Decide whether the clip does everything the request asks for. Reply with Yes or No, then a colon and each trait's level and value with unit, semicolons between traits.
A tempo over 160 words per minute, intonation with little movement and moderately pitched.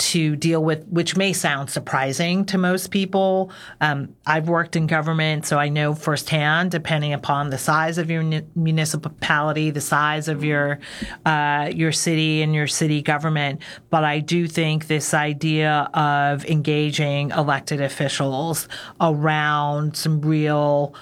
No: average, 145 wpm; narrow, 1.7 semitones; medium, 155 Hz